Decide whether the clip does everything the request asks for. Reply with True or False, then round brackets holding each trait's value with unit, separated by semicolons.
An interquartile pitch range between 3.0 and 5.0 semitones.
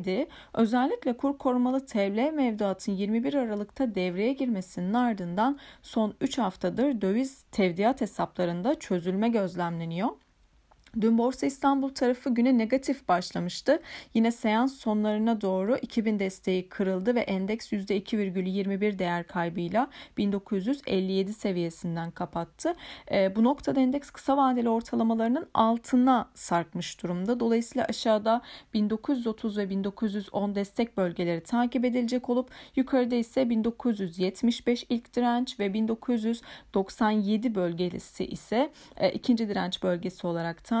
True (4.6 semitones)